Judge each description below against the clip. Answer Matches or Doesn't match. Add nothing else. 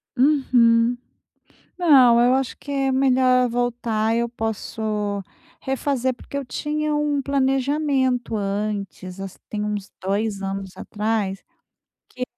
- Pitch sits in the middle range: Doesn't match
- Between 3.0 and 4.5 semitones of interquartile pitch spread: Matches